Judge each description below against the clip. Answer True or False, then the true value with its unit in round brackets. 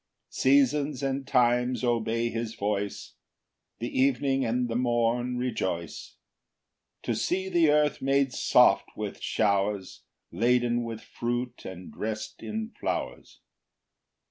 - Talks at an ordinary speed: False (115 wpm)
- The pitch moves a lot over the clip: False (3.0 semitones)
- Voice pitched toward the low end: True (120 Hz)